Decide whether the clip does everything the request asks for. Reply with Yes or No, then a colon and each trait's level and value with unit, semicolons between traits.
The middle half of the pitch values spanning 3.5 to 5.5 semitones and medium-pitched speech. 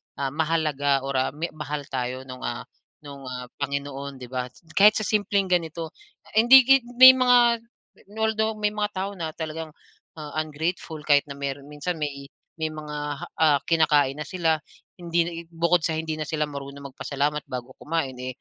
Yes: average, 3.8 semitones; medium, 155 Hz